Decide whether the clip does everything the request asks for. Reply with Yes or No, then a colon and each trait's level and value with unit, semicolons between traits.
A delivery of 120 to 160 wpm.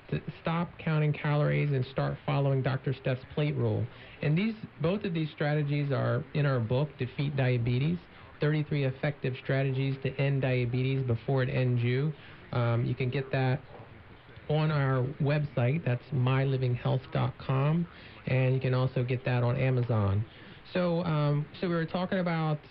Yes: average, 150 wpm